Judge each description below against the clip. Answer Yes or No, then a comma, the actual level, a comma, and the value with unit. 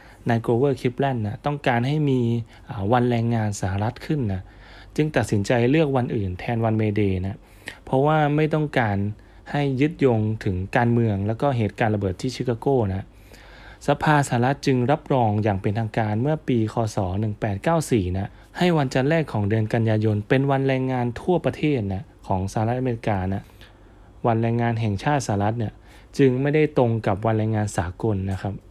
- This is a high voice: No, low, 115 Hz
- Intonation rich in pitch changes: No, average, 4.3 semitones